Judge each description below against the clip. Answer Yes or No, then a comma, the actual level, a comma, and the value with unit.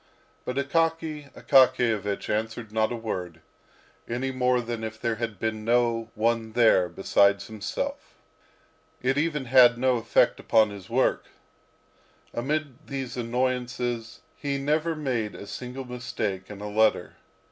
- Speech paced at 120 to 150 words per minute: Yes, slow, 135 wpm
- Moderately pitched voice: No, low, 120 Hz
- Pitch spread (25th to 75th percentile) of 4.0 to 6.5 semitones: No, average, 3.0 semitones